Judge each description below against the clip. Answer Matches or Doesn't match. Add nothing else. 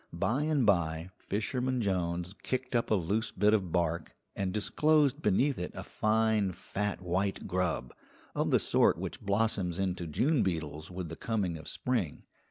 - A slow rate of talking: Doesn't match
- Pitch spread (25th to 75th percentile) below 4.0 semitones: Doesn't match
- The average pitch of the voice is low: Matches